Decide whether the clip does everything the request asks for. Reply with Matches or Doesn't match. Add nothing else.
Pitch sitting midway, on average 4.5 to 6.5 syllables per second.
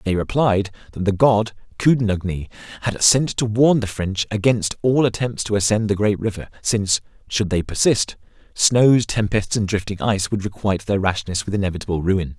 Doesn't match